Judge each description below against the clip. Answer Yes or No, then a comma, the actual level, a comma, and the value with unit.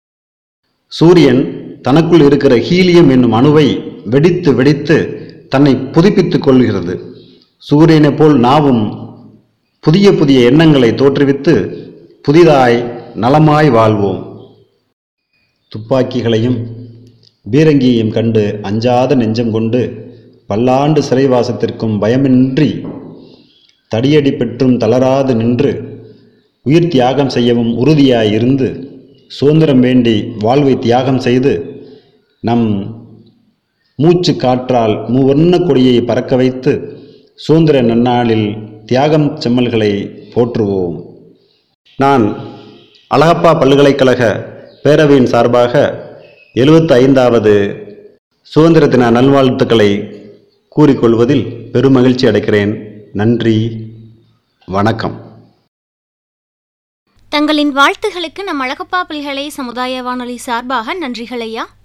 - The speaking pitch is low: Yes, low, 125 Hz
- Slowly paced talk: Yes, slow, 75 wpm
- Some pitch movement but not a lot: Yes, average, 4.6 semitones